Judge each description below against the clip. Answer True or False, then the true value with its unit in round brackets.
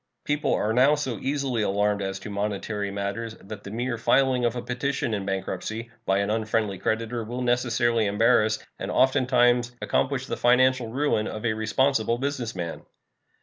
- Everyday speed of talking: True (165 wpm)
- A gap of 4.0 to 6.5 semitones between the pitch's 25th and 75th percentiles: False (3.0 semitones)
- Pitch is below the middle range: True (115 Hz)